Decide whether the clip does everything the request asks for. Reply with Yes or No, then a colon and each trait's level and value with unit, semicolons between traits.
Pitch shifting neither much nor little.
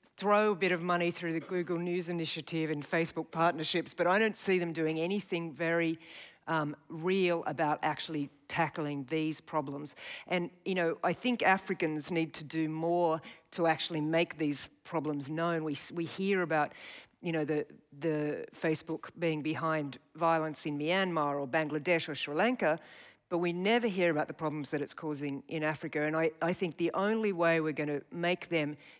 No: narrow, 2.2 semitones